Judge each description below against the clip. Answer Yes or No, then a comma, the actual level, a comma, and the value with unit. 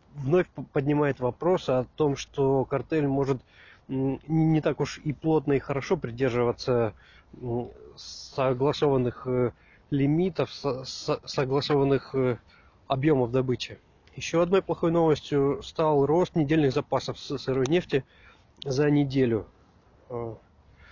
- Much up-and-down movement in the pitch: No, average, 3.2 semitones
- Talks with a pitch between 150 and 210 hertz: No, low, 135 Hz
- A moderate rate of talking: No, slow, 95 wpm